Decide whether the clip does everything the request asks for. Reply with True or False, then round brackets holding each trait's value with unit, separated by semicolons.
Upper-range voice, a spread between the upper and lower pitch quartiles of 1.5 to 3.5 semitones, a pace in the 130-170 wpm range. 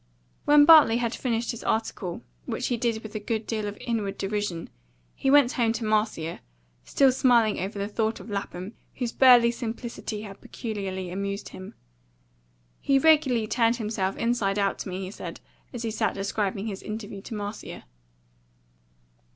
True (220 Hz; 3.0 semitones; 165 wpm)